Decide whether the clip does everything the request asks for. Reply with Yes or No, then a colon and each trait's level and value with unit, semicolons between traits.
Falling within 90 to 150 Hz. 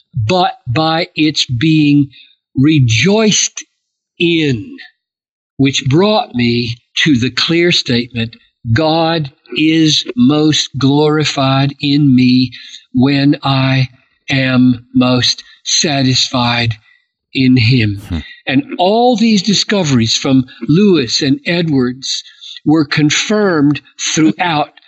Yes: medium, 140 Hz